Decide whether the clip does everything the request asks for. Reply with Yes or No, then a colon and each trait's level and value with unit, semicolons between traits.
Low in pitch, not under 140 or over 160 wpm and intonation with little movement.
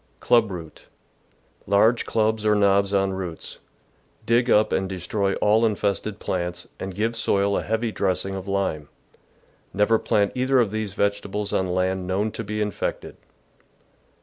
Yes: low, 100 Hz; average, 150 wpm; narrow, 2.2 semitones